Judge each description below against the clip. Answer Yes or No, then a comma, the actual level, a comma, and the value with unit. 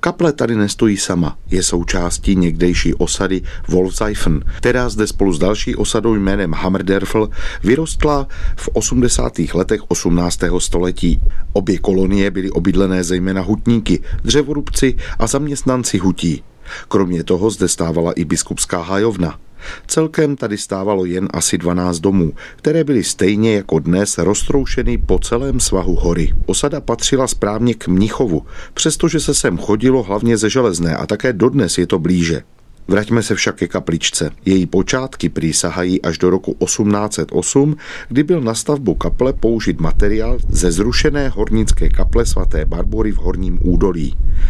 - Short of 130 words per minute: No, average, 140 wpm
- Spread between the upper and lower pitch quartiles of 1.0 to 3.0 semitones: No, average, 4.6 semitones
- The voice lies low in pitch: Yes, very low, 95 Hz